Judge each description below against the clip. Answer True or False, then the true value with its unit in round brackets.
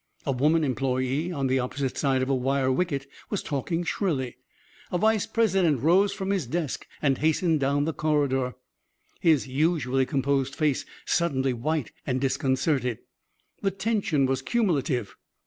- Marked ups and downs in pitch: False (4.3 semitones)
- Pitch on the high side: False (140 Hz)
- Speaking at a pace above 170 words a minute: False (145 wpm)